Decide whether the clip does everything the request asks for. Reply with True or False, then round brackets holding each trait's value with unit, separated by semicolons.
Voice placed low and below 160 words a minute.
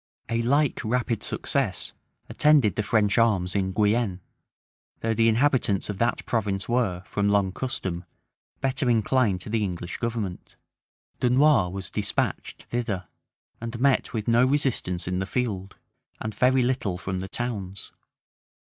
True (110 Hz; 140 wpm)